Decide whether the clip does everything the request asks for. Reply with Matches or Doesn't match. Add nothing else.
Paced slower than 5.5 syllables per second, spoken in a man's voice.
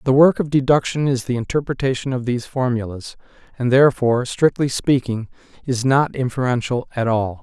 Doesn't match